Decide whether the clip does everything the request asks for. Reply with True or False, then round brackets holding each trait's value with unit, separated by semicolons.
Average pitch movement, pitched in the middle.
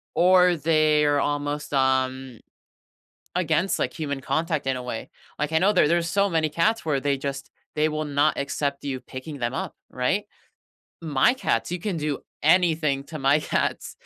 True (3.2 semitones; 150 Hz)